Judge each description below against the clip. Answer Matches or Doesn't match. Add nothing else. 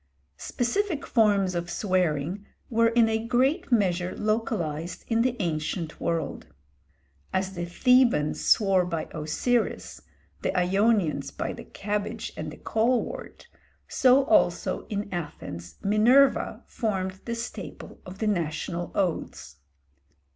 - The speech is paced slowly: Matches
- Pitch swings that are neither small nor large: Matches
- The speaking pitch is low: Doesn't match